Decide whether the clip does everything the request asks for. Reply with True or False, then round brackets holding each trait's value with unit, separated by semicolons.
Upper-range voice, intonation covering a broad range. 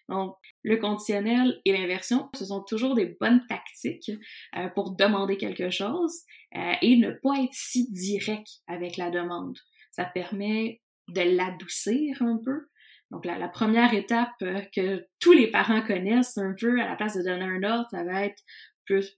False (210 Hz; 3.8 semitones)